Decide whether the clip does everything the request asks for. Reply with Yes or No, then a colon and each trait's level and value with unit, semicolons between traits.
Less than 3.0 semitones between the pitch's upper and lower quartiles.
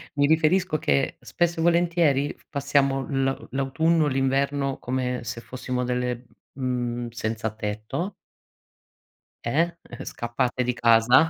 No: average, 3.4 semitones